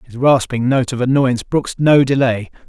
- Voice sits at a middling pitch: No, low, 130 Hz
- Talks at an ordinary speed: Yes, average, 180 wpm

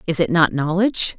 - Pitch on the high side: No, medium, 175 Hz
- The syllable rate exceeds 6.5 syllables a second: No, 5.9 syllables/s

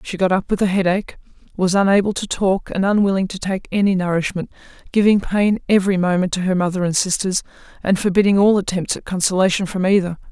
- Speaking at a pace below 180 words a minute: No, average, 190 wpm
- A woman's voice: Yes, female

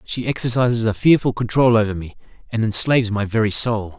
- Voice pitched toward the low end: Yes, low, 110 Hz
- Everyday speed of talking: Yes, average, 180 wpm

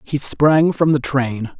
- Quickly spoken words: No, average, 190 wpm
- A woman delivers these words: No, male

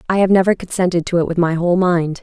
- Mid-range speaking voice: Yes, medium, 175 Hz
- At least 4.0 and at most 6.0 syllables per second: No, 6.8 syllables/s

